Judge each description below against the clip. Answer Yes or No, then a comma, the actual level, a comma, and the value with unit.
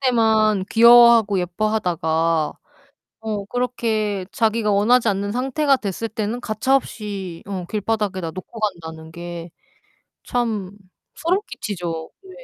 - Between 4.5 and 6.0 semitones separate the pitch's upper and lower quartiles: No, average, 4.1 semitones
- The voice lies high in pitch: Yes, high, 210 Hz